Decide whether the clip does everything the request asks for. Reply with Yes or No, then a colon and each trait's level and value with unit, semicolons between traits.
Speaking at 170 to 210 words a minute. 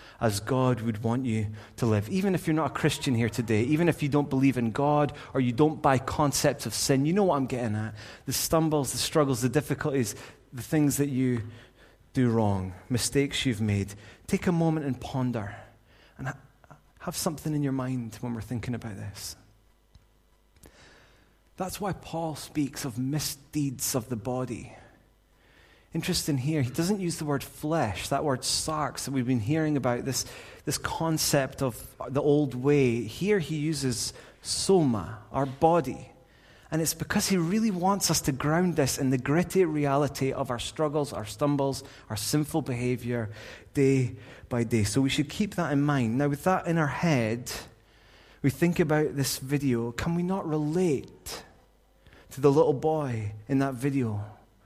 Yes: average, 175 wpm